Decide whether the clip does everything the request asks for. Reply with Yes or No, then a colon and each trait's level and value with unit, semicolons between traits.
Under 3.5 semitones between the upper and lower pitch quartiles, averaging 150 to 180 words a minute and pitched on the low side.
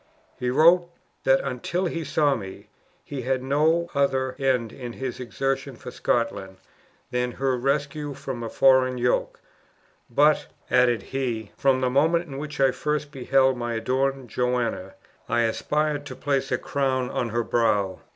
Yes: average, 2.7 semitones; average, 155 wpm; low, 130 Hz